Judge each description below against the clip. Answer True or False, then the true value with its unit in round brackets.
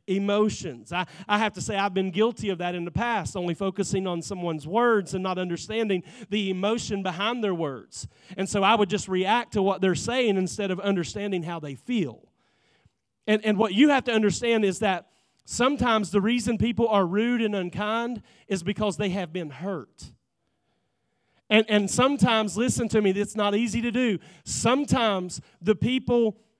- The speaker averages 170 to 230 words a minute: True (180 wpm)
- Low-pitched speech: False (205 Hz)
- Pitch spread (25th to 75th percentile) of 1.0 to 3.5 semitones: True (3.2 semitones)